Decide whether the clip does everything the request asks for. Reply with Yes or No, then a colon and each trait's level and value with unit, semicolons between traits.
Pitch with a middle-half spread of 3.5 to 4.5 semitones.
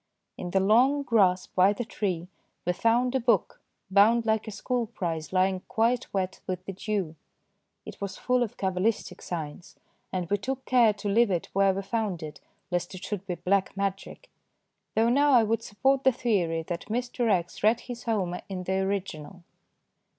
Yes: average, 4.1 semitones